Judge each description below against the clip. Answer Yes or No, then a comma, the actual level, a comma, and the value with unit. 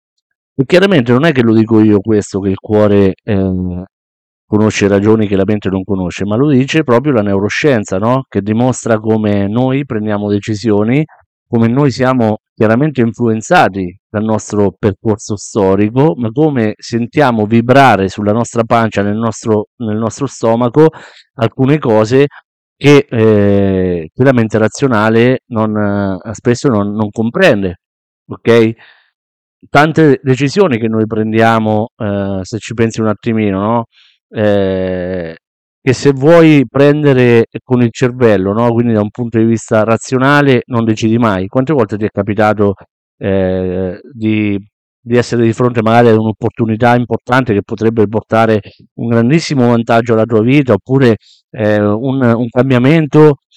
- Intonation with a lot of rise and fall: No, average, 3.1 semitones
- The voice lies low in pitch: Yes, low, 110 Hz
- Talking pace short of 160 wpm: Yes, average, 145 wpm